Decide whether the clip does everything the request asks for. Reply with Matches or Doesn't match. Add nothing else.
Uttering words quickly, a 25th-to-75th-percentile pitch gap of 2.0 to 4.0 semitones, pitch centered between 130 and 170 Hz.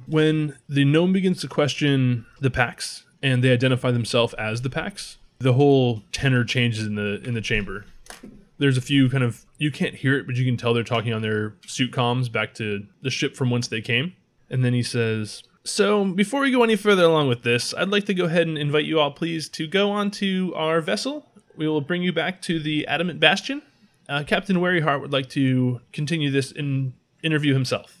Doesn't match